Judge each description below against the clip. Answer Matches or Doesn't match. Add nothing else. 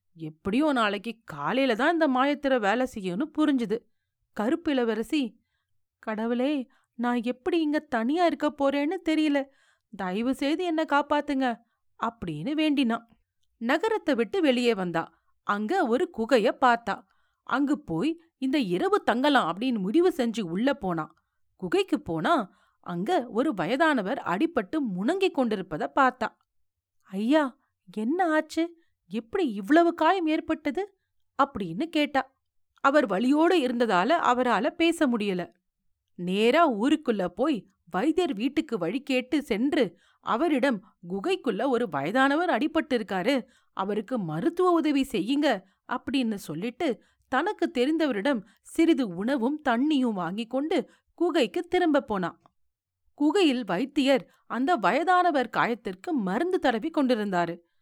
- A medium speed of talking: Doesn't match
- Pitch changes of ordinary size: Doesn't match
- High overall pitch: Matches